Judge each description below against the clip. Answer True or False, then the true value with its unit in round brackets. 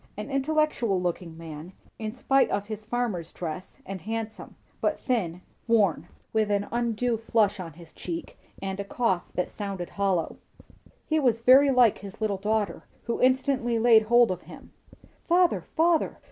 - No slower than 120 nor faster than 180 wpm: True (160 wpm)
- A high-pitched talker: True (215 Hz)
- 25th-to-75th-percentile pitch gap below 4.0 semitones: False (4.5 semitones)